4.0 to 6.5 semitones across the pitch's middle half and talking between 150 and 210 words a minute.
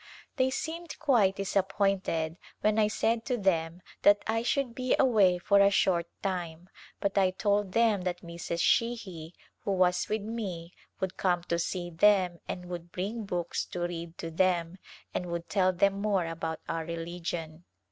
No: average, 3.3 semitones; average, 165 wpm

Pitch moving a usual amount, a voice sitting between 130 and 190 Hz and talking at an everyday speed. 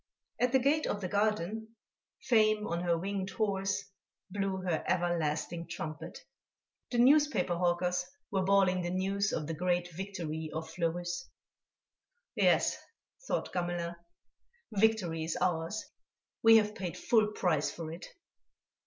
No: average, 3.5 semitones; medium, 185 Hz; slow, 130 wpm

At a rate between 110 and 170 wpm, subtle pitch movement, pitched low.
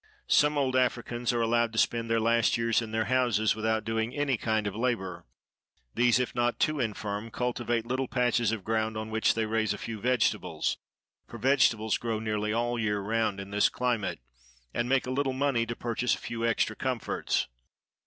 No: average, 185 wpm; narrow, 1.9 semitones; low, 115 Hz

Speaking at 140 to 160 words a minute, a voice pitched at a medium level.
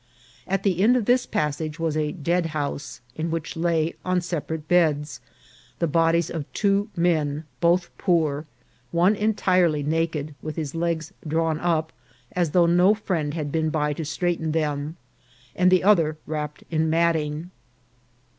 Yes: average, 150 wpm; medium, 165 Hz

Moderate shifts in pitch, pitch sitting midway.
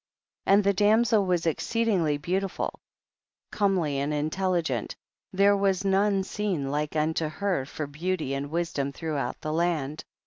Yes: average, 4.7 semitones; medium, 175 Hz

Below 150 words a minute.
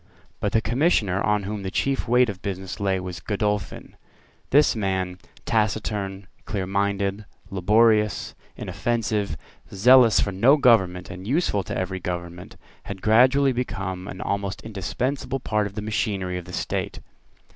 Yes: average, 140 wpm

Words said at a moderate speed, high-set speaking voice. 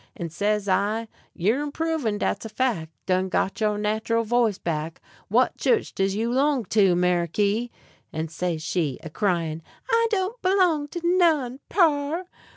Yes: average, 155 wpm; high, 215 Hz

